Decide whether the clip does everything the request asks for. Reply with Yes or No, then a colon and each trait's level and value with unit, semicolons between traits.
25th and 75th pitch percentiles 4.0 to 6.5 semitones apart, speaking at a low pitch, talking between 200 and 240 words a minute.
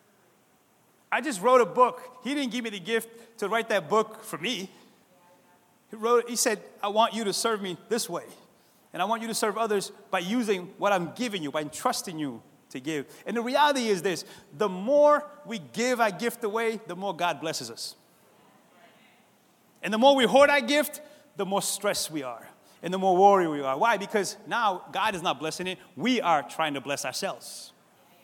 No: average, 4.3 semitones; high, 215 Hz; fast, 205 wpm